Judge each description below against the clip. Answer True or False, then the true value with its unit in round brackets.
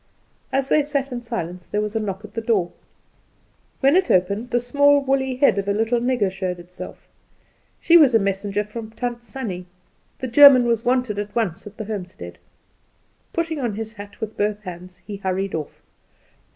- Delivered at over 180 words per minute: True (190 wpm)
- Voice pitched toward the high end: True (220 Hz)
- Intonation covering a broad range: False (4.3 semitones)